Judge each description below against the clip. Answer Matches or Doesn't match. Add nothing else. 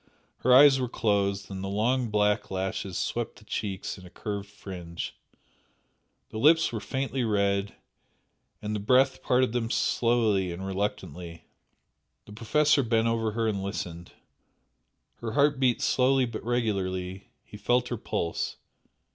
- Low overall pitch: Matches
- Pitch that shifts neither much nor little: Matches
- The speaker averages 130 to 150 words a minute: Matches